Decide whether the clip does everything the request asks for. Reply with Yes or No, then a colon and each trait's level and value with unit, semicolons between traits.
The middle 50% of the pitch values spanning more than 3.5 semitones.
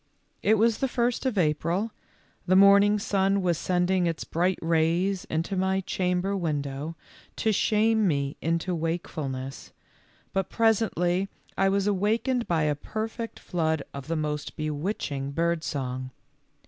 Yes: average, 4.1 semitones